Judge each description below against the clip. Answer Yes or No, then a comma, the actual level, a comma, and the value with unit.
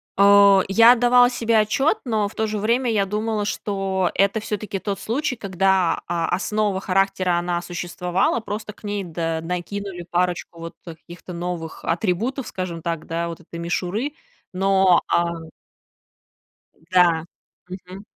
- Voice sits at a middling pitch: No, high, 195 Hz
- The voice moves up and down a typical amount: Yes, average, 3.4 semitones